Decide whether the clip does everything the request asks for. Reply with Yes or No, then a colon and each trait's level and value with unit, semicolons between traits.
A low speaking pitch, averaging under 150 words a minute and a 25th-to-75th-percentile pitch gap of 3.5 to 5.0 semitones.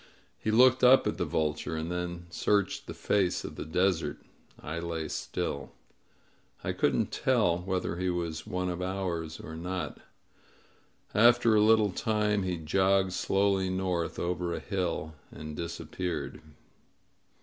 No: very low, 90 Hz; average, 140 wpm; average, 2.7 semitones